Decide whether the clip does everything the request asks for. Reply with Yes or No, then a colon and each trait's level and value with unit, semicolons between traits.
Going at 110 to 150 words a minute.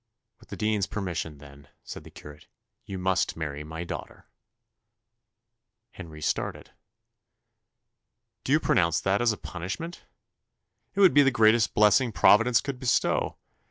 Yes: slow, 135 wpm